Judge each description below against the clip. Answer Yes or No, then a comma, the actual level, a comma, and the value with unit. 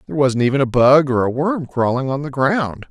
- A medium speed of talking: No, fast, 250 wpm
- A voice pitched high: No, low, 135 Hz